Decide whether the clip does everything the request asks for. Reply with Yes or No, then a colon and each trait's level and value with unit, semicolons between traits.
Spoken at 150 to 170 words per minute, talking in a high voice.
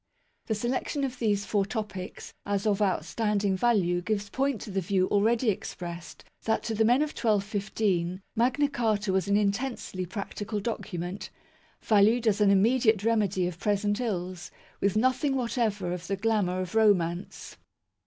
Yes: average, 155 wpm; high, 205 Hz